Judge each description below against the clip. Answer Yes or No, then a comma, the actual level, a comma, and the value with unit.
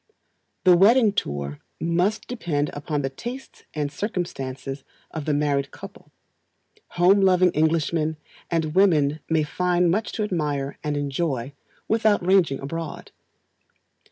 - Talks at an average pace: No, slow, 125 wpm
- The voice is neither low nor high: Yes, medium, 160 Hz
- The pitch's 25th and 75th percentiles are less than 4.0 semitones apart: No, average, 4.3 semitones